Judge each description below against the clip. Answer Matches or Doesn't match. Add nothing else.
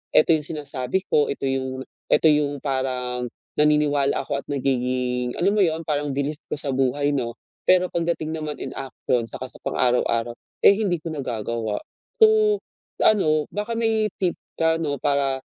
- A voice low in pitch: Doesn't match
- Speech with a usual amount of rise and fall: Matches